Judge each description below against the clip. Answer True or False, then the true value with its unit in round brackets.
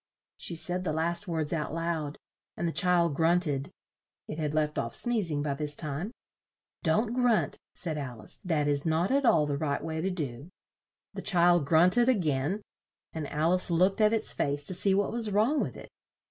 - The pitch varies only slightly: False (4.2 semitones)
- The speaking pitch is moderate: True (165 Hz)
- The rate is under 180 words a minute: False (205 wpm)